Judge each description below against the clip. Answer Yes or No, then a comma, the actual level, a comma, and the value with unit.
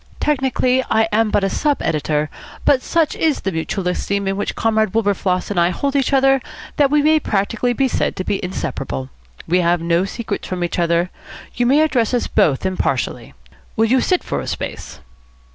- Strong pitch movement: Yes, wide, 6.7 semitones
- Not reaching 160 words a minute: No, average, 195 wpm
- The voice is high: Yes, high, 210 Hz